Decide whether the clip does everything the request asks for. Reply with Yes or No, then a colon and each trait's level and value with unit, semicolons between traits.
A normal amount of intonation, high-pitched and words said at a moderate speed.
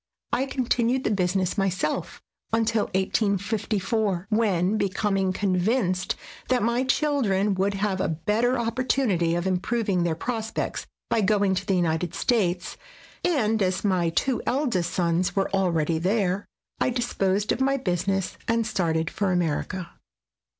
Yes: average, 3.9 semitones; high, 195 Hz; average, 145 wpm